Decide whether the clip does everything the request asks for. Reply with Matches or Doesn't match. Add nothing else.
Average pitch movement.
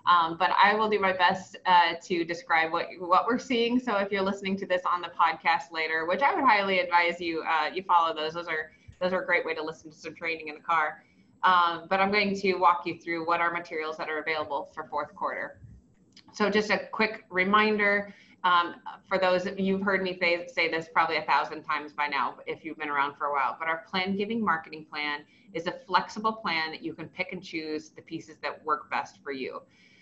Matches